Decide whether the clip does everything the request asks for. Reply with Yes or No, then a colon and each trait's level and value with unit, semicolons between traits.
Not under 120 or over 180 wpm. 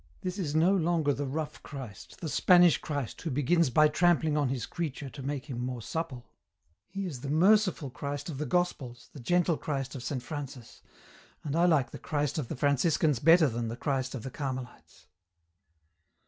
No: average, 190 wpm